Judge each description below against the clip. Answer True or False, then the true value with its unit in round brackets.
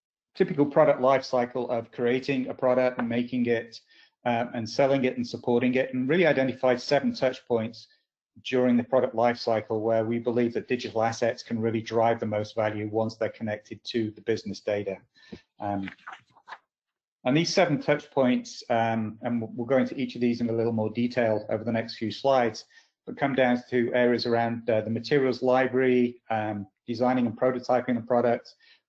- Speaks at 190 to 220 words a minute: False (180 wpm)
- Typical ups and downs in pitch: False (2.1 semitones)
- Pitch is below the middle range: True (120 Hz)